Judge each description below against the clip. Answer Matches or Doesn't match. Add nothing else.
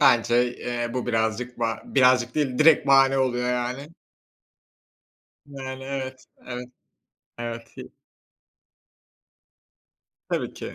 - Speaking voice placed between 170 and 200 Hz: Doesn't match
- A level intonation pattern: Matches